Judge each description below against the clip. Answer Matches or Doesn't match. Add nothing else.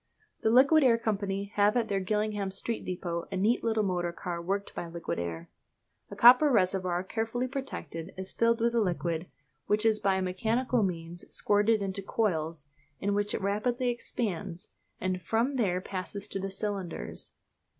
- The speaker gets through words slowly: Doesn't match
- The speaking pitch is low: Doesn't match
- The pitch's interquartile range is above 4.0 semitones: Doesn't match